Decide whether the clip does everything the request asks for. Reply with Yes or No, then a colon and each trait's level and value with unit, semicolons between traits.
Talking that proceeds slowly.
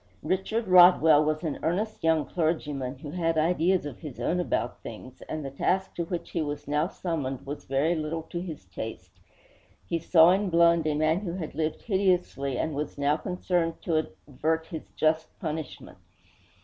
No: average, 175 wpm